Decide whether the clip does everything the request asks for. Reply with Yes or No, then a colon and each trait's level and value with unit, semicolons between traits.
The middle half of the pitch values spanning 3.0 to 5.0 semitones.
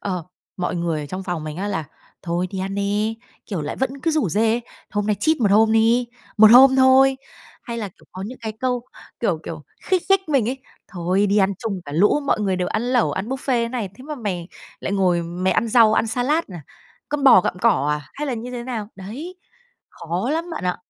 No: wide, 5.5 semitones